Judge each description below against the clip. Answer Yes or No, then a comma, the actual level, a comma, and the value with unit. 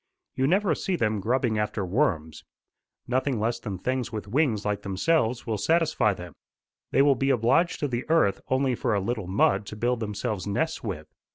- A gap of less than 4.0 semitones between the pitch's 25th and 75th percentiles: No, average, 4.8 semitones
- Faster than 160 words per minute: Yes, average, 185 wpm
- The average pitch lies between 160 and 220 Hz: No, low, 115 Hz